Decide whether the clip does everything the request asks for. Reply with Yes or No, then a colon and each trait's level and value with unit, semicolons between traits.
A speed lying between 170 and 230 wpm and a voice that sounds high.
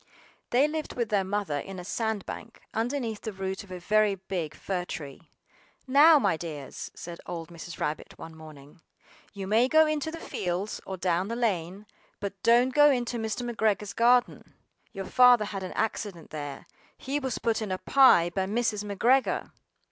Yes: average, 180 wpm; high, 205 Hz